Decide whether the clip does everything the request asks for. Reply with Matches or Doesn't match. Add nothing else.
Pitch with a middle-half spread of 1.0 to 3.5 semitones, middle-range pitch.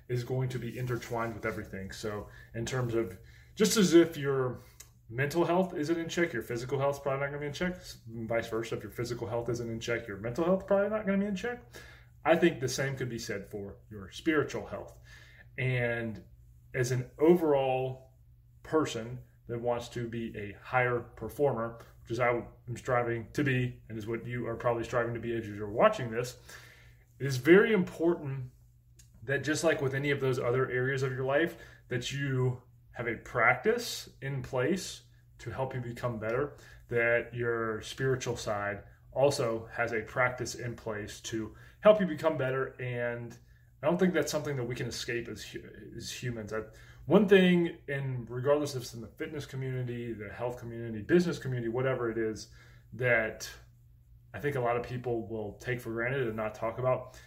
Doesn't match